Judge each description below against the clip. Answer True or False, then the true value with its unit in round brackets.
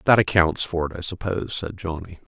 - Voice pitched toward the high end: False (90 Hz)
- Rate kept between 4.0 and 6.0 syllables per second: True (5.9 syllables/s)